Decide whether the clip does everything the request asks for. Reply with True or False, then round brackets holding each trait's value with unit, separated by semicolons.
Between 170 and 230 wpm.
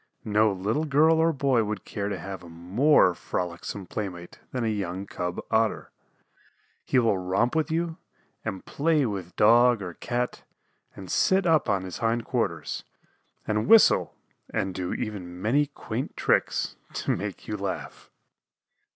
False (150 wpm)